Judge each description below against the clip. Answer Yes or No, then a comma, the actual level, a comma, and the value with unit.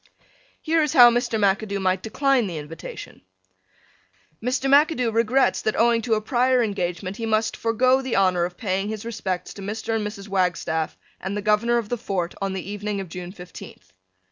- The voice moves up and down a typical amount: Yes, average, 3.8 semitones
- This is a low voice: No, high, 210 Hz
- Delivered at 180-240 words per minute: Yes, average, 185 wpm